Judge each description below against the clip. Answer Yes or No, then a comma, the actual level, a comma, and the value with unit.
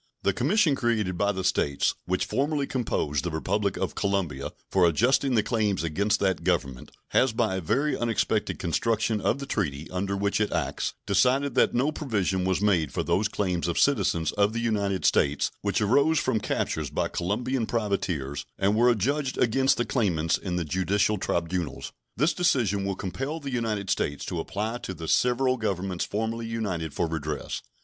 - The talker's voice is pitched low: Yes, low, 100 Hz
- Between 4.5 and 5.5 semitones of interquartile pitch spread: Yes, average, 4.9 semitones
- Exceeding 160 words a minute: Yes, average, 175 wpm